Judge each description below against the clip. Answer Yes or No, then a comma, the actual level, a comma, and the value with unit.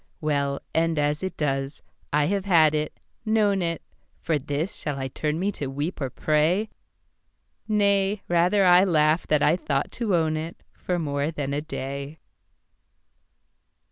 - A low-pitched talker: No, medium, 155 Hz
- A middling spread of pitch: Yes, average, 4.0 semitones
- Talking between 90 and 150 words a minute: Yes, average, 140 wpm